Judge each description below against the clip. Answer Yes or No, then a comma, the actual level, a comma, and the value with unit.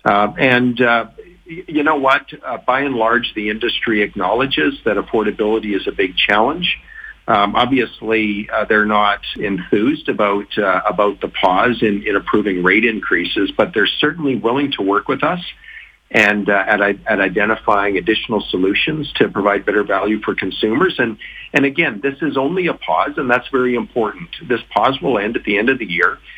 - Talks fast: No, average, 175 wpm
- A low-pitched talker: Yes, low, 110 Hz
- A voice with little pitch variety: No, average, 3.6 semitones